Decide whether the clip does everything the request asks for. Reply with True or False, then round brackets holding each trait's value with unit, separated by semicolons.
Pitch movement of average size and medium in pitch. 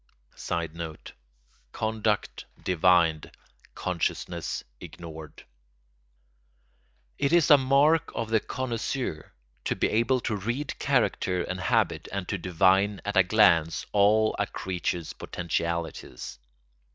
False (4.8 semitones; 95 Hz)